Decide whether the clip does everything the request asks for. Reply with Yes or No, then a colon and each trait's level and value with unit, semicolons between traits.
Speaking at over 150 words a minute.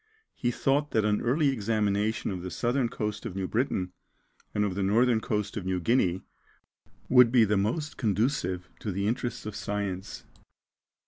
Yes: average, 170 wpm